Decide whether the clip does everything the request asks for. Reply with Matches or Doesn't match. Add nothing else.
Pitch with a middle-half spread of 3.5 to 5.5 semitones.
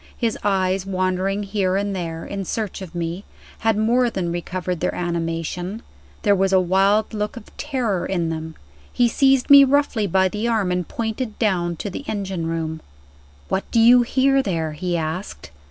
Matches